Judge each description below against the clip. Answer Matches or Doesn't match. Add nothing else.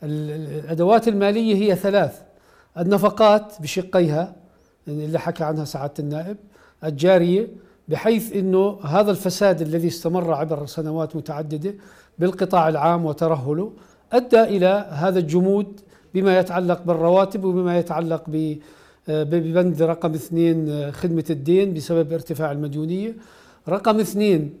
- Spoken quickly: Doesn't match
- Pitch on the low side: Doesn't match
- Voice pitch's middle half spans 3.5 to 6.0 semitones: Matches